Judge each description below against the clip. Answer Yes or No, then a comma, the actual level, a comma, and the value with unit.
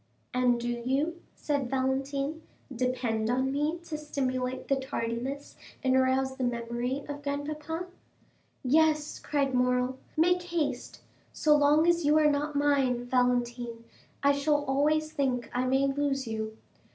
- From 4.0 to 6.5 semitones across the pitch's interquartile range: No, average, 2.9 semitones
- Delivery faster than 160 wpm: No, average, 140 wpm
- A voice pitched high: Yes, very high, 270 Hz